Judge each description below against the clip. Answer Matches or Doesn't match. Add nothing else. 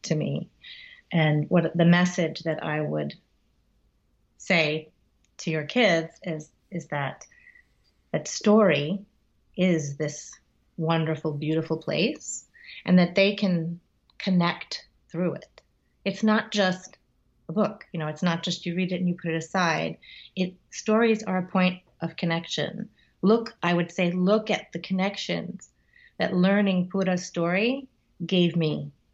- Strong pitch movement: Doesn't match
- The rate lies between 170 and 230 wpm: Doesn't match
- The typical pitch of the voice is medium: Matches